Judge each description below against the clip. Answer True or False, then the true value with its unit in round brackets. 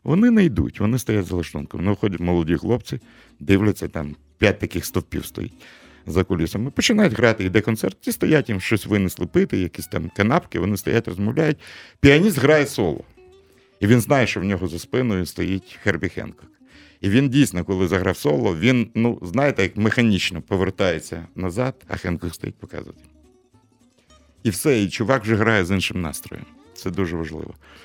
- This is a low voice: True (100 Hz)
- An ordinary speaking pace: False (170 wpm)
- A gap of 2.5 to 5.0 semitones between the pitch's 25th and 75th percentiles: False (5.4 semitones)